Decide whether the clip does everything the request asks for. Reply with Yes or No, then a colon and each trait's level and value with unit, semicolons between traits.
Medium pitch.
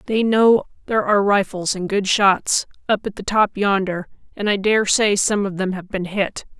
No: high, 200 Hz